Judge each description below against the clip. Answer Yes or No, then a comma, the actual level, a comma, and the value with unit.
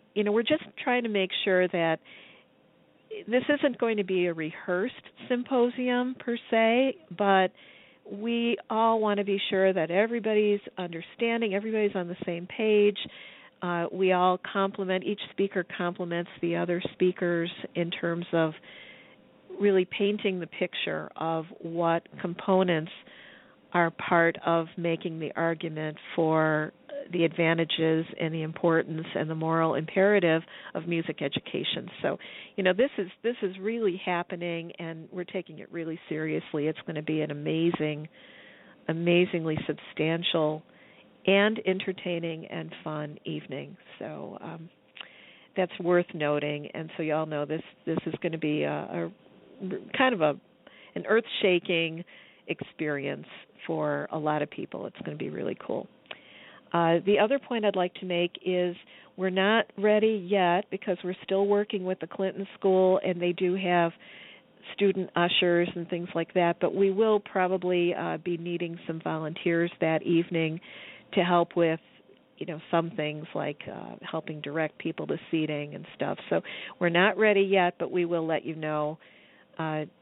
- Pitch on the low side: No, medium, 175 Hz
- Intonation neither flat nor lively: Yes, average, 3.5 semitones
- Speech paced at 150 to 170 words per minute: Yes, average, 155 wpm